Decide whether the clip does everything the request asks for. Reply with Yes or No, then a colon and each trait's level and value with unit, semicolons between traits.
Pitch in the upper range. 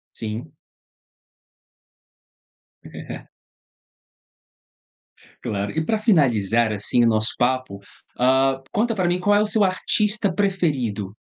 No: low, 135 Hz